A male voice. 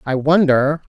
No: female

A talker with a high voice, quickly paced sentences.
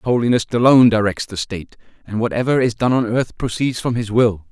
No: low, 115 Hz; fast, 215 wpm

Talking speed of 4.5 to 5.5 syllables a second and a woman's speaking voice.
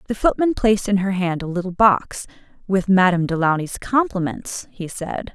Yes: 5.1 syllables/s; female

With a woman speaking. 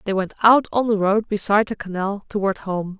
Yes: female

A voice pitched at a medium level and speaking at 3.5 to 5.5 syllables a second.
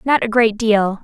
No: high, 220 Hz; 4.3 syllables/s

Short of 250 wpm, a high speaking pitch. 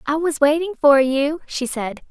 Yes: average, 200 wpm; very high, 290 Hz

